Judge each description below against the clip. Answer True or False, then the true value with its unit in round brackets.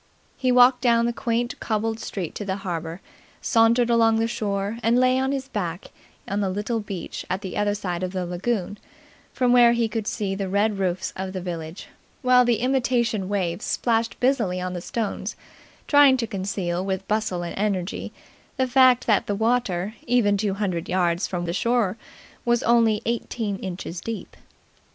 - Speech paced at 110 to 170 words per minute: False (180 wpm)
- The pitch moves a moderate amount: True (4.1 semitones)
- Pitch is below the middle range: False (210 Hz)